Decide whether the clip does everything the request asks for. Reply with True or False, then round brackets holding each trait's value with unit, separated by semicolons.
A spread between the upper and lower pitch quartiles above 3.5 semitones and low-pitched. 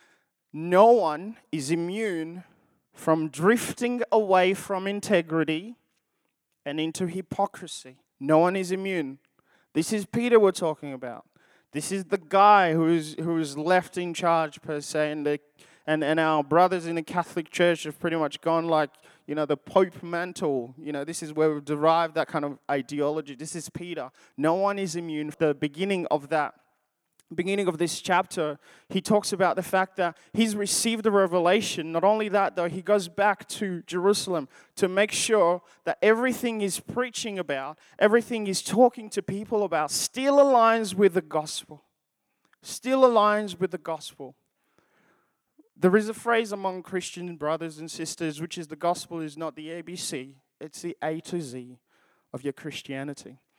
False (4.2 semitones; 175 Hz)